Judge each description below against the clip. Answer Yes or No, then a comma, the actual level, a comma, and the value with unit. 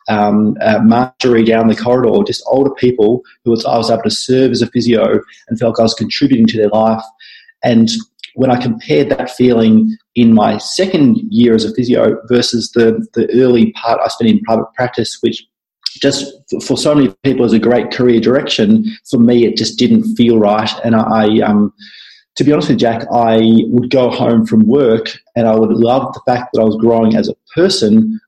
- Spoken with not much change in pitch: No, average, 3.9 semitones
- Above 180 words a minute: Yes, fast, 205 wpm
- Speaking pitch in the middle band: No, low, 120 Hz